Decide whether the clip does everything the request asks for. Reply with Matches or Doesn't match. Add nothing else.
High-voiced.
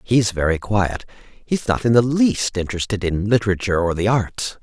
Doesn't match